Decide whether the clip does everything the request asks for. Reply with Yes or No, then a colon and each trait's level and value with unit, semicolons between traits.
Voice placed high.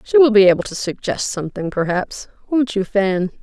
Yes: high, 210 Hz